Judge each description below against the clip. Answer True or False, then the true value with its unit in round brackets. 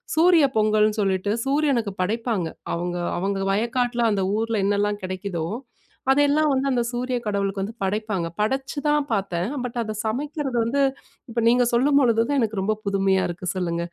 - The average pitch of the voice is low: False (220 Hz)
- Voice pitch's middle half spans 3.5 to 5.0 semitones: True (4.6 semitones)